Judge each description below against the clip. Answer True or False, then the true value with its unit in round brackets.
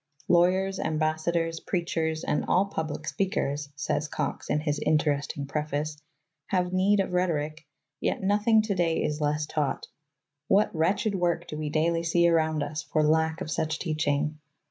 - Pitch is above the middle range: False (160 Hz)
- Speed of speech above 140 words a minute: True (155 wpm)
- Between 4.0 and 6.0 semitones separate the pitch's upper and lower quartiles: False (2.8 semitones)